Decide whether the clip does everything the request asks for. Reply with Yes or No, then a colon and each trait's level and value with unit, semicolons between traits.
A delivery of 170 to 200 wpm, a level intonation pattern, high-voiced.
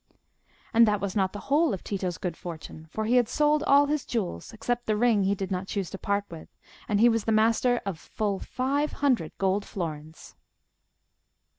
No: average, 190 wpm; average, 4.3 semitones; high, 210 Hz